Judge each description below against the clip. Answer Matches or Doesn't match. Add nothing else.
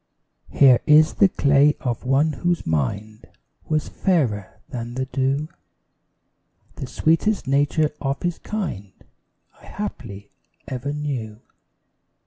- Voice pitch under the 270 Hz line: Matches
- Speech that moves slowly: Matches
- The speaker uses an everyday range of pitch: Matches